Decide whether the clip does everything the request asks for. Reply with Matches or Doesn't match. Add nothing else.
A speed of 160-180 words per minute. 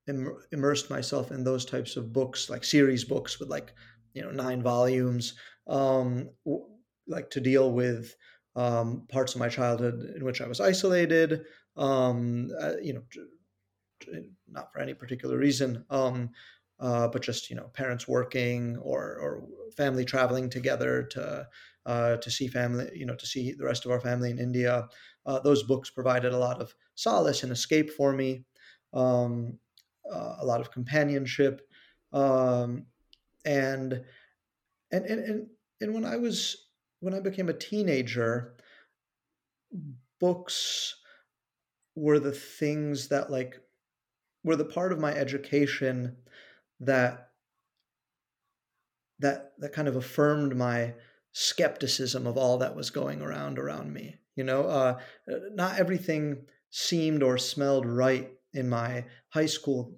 Doesn't match